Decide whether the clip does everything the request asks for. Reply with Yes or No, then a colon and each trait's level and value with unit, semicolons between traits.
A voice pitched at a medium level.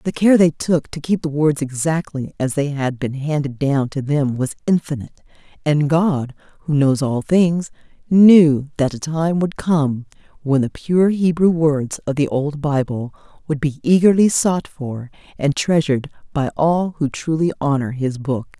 Yes: medium, 150 Hz